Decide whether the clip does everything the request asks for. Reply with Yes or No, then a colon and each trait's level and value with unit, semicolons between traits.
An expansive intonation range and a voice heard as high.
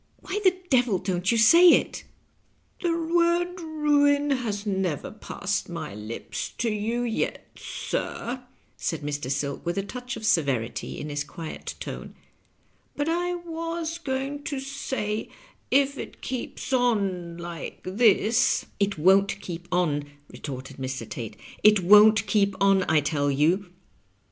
Yes: wide, 8.5 semitones; high, 210 Hz